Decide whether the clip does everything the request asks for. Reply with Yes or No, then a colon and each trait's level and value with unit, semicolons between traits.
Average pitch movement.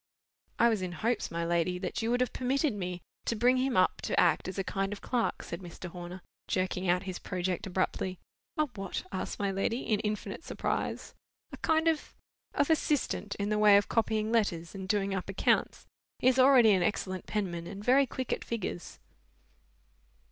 Yes: average, 4.2 semitones